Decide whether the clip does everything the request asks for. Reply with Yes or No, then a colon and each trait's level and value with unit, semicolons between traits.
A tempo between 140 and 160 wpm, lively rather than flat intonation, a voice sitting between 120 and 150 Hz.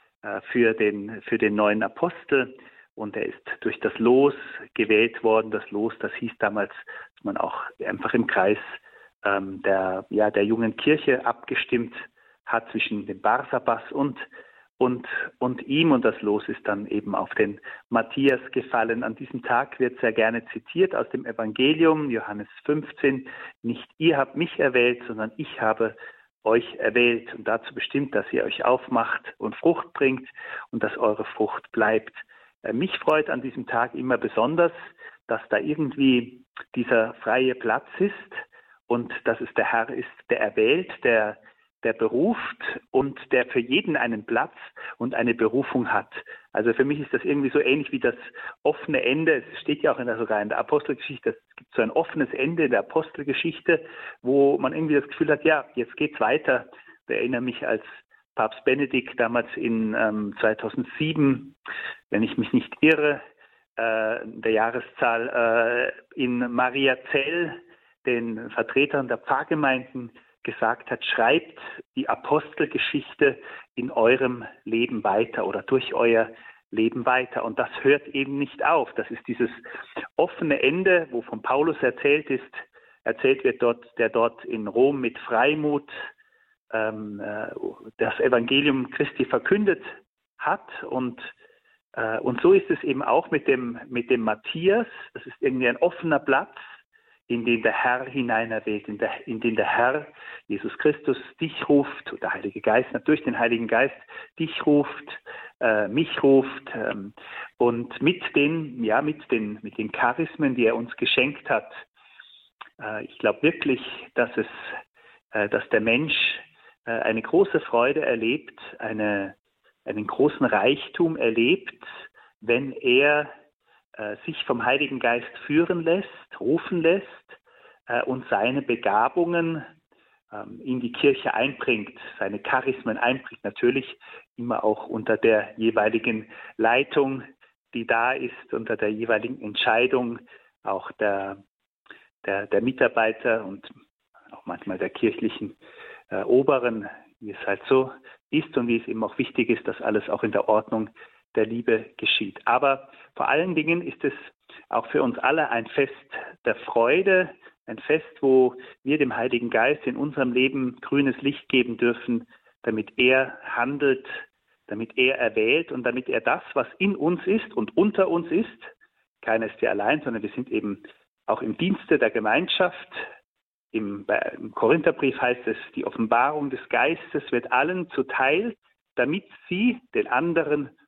Yes: average, 150 wpm; wide, 6.6 semitones; low, 135 Hz